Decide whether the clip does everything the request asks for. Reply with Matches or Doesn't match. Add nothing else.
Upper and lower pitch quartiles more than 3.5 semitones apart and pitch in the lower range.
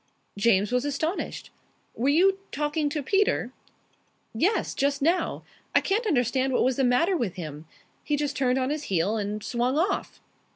Doesn't match